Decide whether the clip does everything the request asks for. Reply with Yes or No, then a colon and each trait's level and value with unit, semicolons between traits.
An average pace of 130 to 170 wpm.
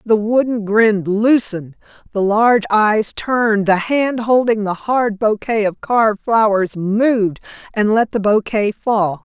Yes: average, 150 wpm